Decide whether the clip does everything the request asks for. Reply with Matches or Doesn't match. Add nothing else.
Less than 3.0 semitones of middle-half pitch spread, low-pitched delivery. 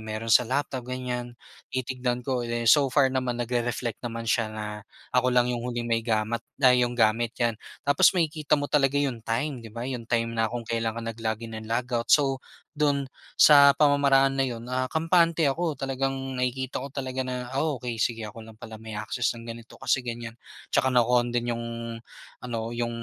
Matches